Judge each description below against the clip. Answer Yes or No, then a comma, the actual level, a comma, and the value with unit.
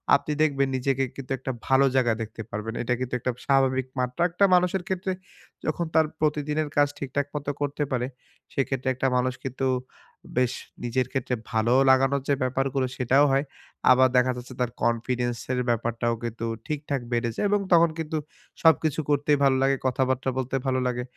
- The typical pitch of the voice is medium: No, low, 130 Hz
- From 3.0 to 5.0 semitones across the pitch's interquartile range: No, narrow, 2.6 semitones